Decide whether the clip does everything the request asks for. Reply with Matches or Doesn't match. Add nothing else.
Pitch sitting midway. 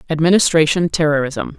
Matches